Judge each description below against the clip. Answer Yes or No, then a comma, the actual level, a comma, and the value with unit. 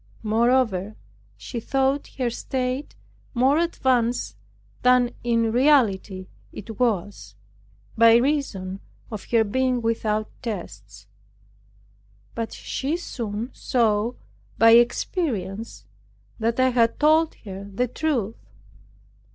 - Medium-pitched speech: No, high, 230 Hz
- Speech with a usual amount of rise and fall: Yes, average, 3.7 semitones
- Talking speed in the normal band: No, slow, 100 wpm